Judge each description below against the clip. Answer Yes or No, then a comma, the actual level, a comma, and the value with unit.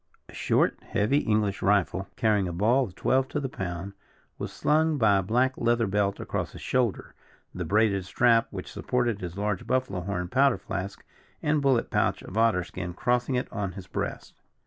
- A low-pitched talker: Yes, low, 105 Hz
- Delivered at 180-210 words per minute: Yes, average, 185 wpm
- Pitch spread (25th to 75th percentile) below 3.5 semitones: No, average, 4.6 semitones